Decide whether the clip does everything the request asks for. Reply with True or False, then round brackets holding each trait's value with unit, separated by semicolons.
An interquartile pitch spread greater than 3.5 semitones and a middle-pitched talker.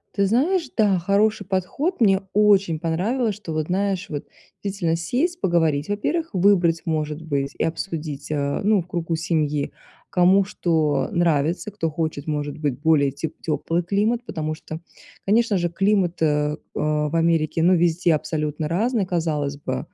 True (4.4 semitones; 170 Hz)